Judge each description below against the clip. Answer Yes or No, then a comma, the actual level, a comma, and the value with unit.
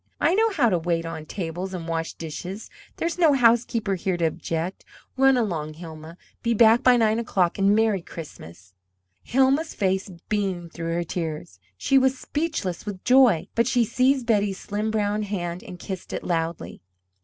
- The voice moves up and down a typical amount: No, wide, 5.8 semitones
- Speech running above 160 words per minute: Yes, average, 170 wpm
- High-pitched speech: Yes, high, 195 Hz